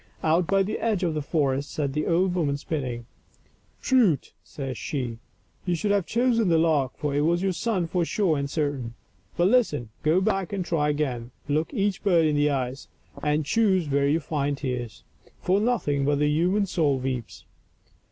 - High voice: No, medium, 155 Hz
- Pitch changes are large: No, average, 4.8 semitones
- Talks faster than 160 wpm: Yes, average, 195 wpm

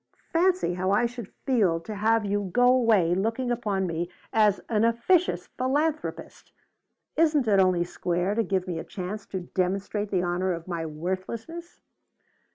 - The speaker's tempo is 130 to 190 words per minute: Yes, average, 160 wpm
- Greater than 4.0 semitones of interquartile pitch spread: Yes, average, 4.8 semitones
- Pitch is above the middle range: Yes, high, 205 Hz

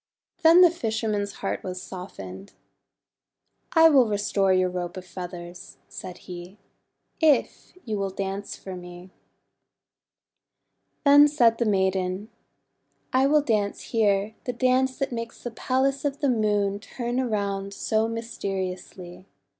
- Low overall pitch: No, high, 205 Hz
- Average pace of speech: No, slow, 130 wpm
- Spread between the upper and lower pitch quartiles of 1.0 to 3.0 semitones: No, average, 5.0 semitones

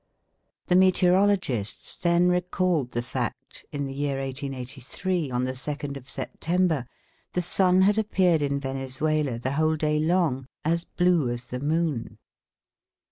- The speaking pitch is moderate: Yes, medium, 150 Hz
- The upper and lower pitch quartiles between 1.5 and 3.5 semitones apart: No, average, 5.1 semitones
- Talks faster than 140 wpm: No, slow, 135 wpm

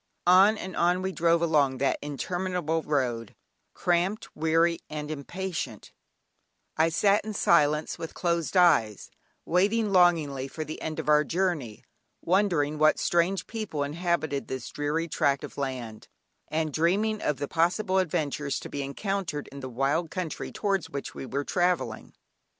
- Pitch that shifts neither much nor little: Yes, average, 4.1 semitones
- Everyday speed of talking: Yes, average, 150 wpm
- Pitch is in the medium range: Yes, medium, 160 Hz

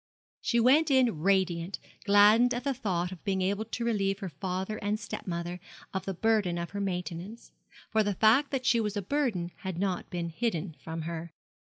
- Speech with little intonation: No, average, 4.1 semitones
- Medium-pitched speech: No, high, 195 Hz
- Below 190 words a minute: No, average, 195 wpm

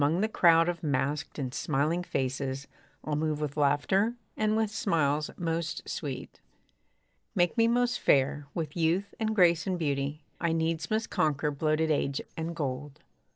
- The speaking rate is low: No, average, 155 wpm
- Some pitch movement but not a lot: Yes, average, 3.4 semitones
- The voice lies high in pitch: No, medium, 160 Hz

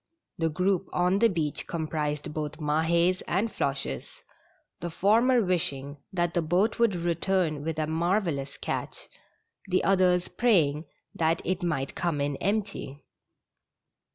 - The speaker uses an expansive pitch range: No, average, 3.6 semitones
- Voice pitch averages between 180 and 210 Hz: No, medium, 170 Hz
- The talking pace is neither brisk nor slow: No, slow, 130 wpm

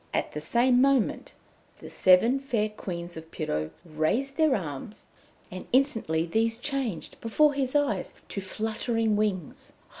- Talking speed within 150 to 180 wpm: No, average, 140 wpm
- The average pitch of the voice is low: No, high, 220 Hz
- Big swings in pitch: Yes, wide, 7.0 semitones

